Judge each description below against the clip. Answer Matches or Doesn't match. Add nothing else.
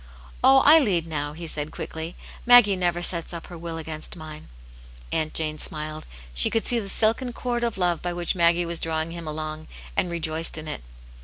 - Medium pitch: Matches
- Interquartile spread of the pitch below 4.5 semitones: Matches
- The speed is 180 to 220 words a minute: Matches